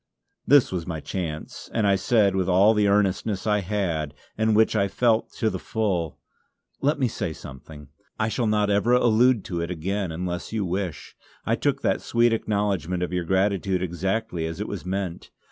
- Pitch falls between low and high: No, low, 100 Hz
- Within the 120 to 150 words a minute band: No, average, 185 wpm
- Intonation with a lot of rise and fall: No, average, 3.6 semitones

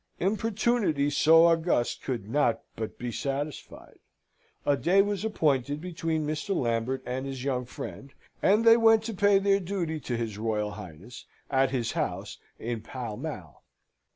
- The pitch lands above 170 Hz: No, medium, 145 Hz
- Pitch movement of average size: No, wide, 7.8 semitones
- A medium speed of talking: Yes, average, 155 wpm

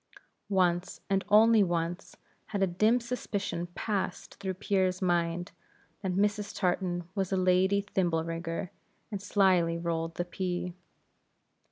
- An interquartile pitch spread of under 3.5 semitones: Yes, narrow, 2.4 semitones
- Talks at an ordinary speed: No, slow, 130 wpm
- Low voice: No, medium, 185 Hz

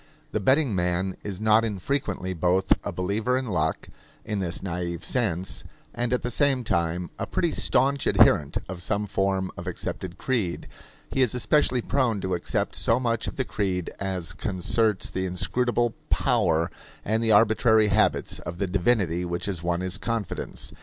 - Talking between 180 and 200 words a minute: No, average, 165 wpm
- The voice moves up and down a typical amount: Yes, average, 4.3 semitones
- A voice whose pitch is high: No, low, 100 Hz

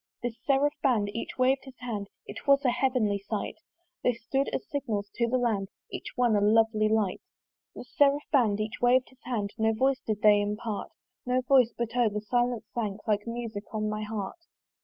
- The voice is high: Yes, high, 230 Hz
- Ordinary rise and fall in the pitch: Yes, average, 3.3 semitones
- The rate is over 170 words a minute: Yes, average, 195 wpm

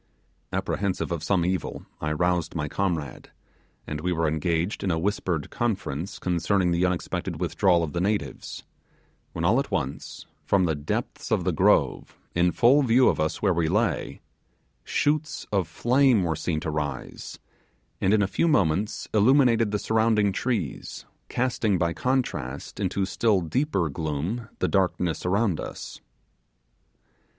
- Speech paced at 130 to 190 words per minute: Yes, average, 150 wpm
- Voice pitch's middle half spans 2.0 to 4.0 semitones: No, average, 4.7 semitones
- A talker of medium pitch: No, very low, 95 Hz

